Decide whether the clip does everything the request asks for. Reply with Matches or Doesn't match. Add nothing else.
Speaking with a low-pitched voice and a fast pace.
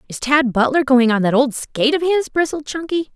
Doesn't match